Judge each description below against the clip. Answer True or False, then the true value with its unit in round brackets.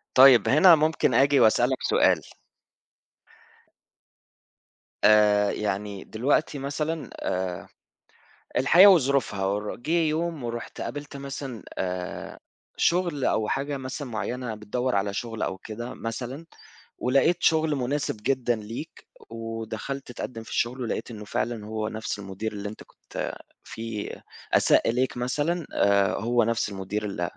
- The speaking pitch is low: True (120 Hz)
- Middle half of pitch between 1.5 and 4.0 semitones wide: False (4.6 semitones)